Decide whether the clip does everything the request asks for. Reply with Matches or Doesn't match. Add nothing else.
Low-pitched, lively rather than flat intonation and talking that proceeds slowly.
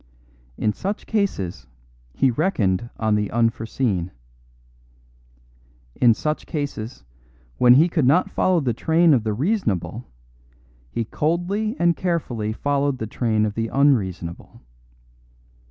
Matches